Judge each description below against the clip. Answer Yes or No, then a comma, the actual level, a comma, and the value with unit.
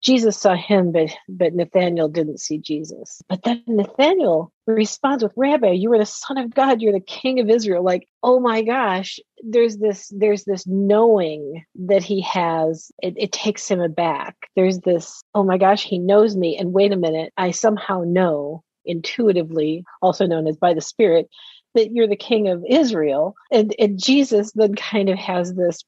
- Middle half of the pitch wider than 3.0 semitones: Yes, average, 3.9 semitones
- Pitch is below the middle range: No, high, 195 Hz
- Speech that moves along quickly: No, average, 185 wpm